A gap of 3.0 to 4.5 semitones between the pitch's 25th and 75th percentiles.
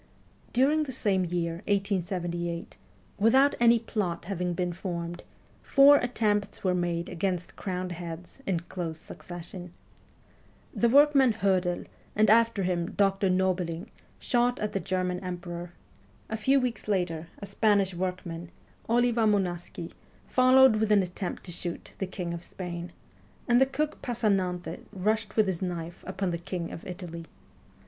Yes: average, 3.8 semitones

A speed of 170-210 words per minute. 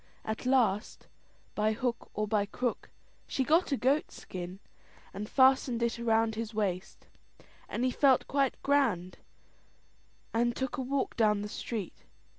No: average, 145 wpm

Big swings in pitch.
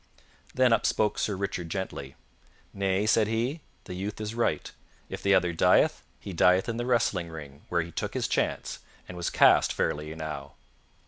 No: average, 4.9 semitones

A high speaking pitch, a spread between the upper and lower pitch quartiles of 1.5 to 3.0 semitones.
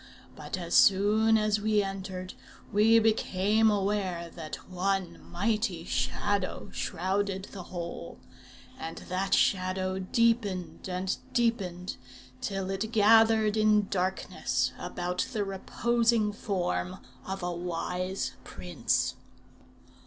Yes: high, 195 Hz; average, 2.7 semitones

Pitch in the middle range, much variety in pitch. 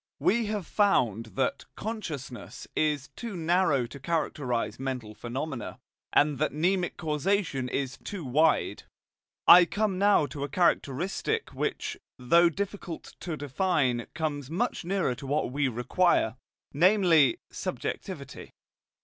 Yes: medium, 155 Hz; wide, 5.8 semitones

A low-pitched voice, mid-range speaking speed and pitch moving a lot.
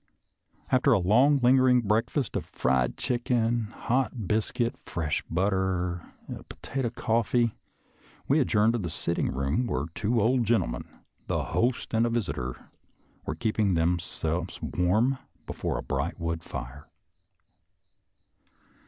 No: low, 110 Hz; slow, 130 wpm; wide, 5.9 semitones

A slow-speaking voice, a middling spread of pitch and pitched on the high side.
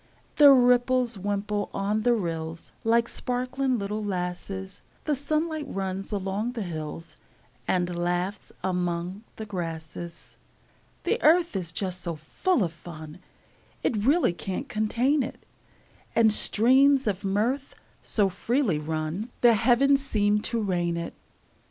No: slow, 130 wpm; wide, 5.7 semitones; high, 205 Hz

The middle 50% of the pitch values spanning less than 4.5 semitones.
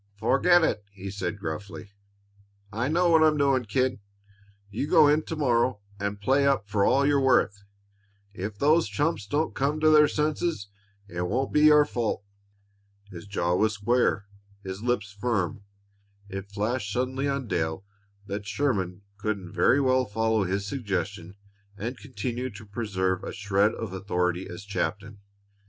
No: average, 5.3 semitones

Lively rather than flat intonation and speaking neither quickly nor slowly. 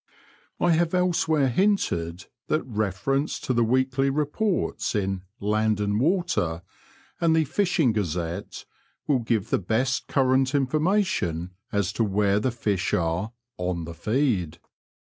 No: wide, 7.6 semitones; slow, 130 wpm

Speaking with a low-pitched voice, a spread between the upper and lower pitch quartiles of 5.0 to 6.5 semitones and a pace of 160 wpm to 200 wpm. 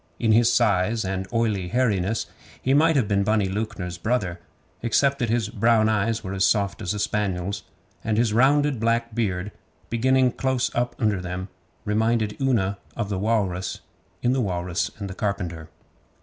No: low, 110 Hz; average, 3.5 semitones; average, 165 wpm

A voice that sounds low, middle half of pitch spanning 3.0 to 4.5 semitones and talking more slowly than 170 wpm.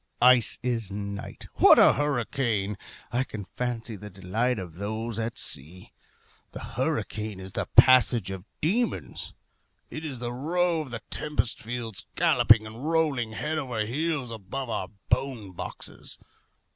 Yes: low, 120 Hz; average, 4.2 semitones; average, 145 wpm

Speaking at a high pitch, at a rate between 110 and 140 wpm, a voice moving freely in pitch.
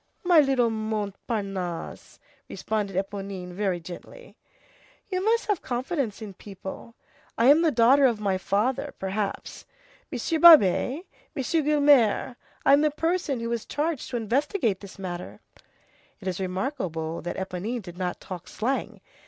Yes: high, 225 Hz; slow, 135 wpm; wide, 6.8 semitones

